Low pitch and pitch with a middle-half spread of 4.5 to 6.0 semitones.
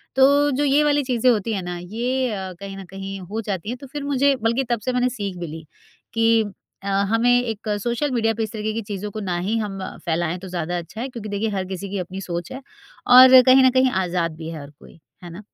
No: high, 215 Hz; average, 5.2 semitones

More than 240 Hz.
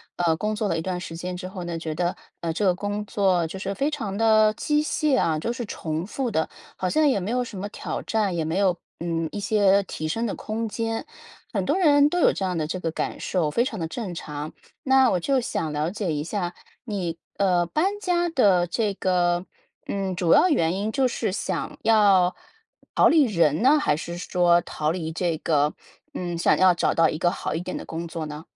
No: medium, 185 Hz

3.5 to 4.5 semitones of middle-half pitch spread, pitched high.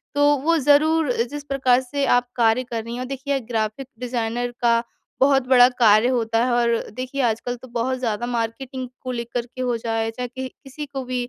No: narrow, 2.4 semitones; very high, 250 Hz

